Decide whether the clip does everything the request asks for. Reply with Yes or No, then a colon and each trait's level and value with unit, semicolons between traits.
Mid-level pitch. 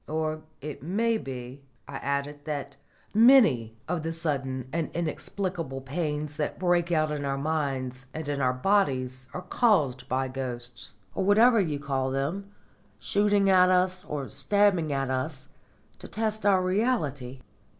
Yes: medium, 150 Hz